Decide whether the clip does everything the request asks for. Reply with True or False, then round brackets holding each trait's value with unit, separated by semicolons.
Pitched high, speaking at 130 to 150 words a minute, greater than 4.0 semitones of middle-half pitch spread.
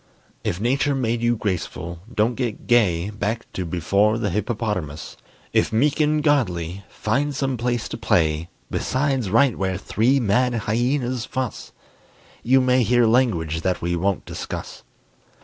False (115 Hz; 145 wpm; 5.1 semitones)